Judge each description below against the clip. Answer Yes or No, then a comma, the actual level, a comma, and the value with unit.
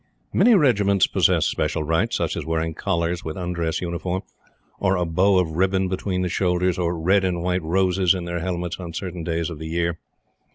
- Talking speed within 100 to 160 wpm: No, average, 195 wpm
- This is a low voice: Yes, very low, 90 Hz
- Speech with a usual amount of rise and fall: No, narrow, 2.0 semitones